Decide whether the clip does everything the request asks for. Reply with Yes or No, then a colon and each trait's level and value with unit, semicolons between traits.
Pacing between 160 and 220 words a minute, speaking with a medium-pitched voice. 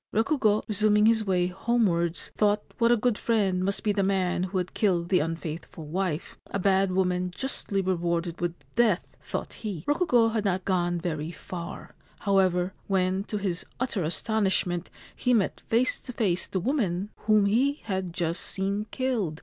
No: average, 165 wpm; high, 195 Hz